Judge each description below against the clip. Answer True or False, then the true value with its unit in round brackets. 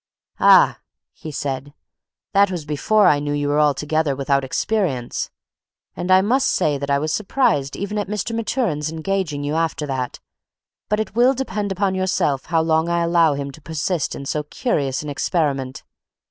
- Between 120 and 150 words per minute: False (175 wpm)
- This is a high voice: False (160 Hz)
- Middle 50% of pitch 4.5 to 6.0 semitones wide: True (5.3 semitones)